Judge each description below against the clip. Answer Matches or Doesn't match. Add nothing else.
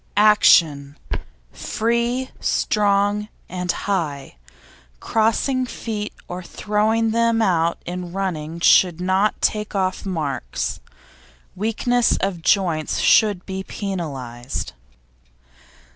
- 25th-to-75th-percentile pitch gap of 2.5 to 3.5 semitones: Doesn't match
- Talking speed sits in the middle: Doesn't match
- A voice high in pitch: Matches